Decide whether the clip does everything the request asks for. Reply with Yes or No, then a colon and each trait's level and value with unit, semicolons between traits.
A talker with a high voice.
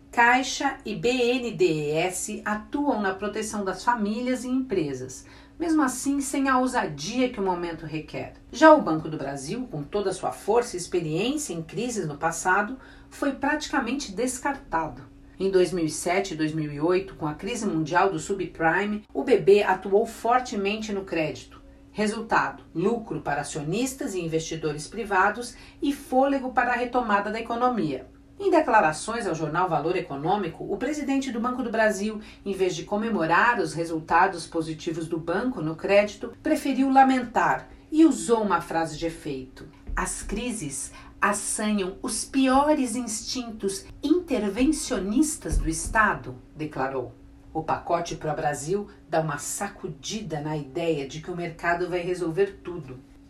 Yes: high, 195 Hz